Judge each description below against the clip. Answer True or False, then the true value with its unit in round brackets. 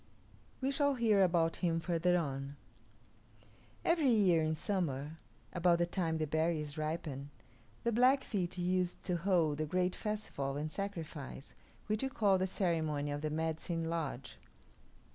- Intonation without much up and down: False (3.7 semitones)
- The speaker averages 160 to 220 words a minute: False (145 wpm)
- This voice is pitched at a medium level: True (170 Hz)